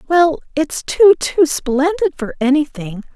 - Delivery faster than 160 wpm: No, slow, 135 wpm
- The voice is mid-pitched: No, very high, 305 Hz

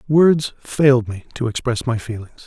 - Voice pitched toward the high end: No, low, 125 Hz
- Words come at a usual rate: Yes, average, 170 wpm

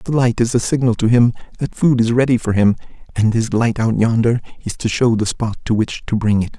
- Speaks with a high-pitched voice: No, low, 115 Hz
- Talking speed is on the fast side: Yes, fast, 255 wpm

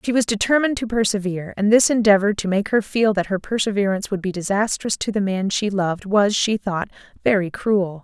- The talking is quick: Yes, fast, 210 wpm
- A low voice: No, high, 205 Hz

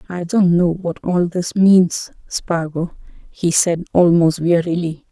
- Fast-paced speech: No, average, 140 wpm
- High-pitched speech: No, medium, 175 Hz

